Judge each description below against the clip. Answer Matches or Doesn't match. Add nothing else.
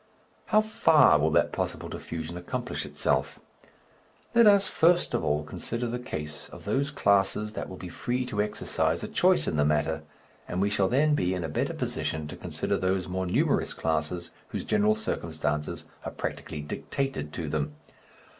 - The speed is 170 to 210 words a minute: Matches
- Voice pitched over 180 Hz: Doesn't match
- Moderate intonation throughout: Doesn't match